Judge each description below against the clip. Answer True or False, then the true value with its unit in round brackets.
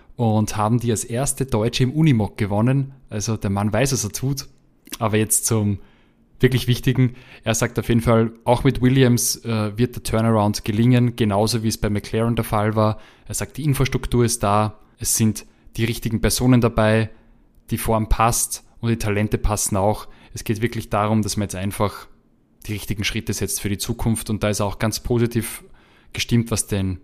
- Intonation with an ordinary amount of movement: False (2.3 semitones)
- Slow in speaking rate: False (190 wpm)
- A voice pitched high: False (110 Hz)